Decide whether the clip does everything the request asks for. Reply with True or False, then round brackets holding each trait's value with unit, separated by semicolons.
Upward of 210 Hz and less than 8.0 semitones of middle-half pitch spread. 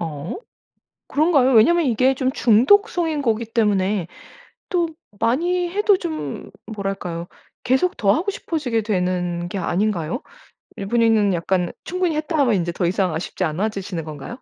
False (220 Hz; 8.8 semitones)